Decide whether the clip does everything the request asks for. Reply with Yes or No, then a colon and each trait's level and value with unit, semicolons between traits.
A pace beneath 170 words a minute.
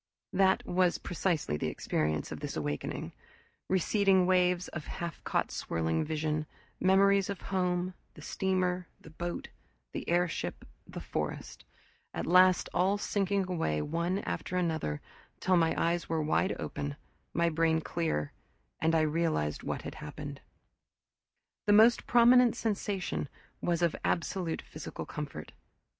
Yes: slow, 135 wpm